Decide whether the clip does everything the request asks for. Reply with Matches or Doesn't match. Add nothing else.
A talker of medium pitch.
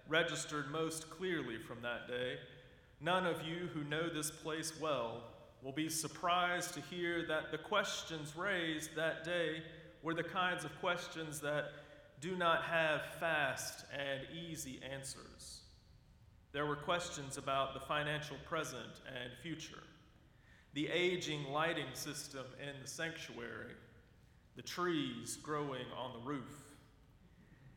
Matches